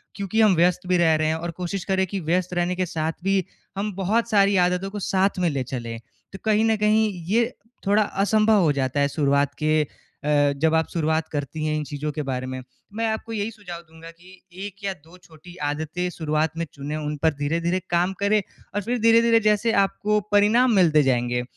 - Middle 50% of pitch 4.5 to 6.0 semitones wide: Yes, average, 4.8 semitones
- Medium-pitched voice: Yes, medium, 175 Hz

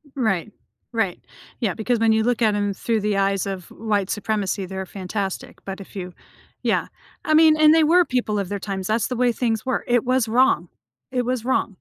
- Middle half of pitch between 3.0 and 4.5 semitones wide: Yes, average, 3.9 semitones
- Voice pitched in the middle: No, high, 220 Hz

